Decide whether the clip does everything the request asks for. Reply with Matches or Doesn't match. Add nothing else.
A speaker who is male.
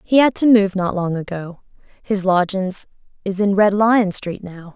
Doesn't match